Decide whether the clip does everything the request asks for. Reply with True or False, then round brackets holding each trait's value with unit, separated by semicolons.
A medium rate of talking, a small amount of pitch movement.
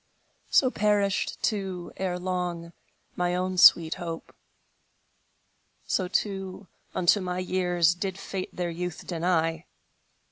False (105 wpm; 1.6 semitones)